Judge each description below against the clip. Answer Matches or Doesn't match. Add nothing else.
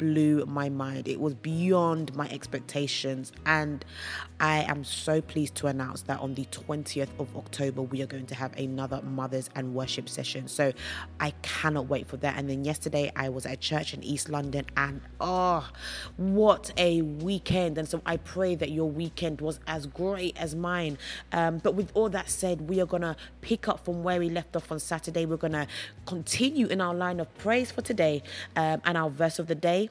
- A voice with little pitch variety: Doesn't match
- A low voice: Doesn't match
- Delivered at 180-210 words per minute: Matches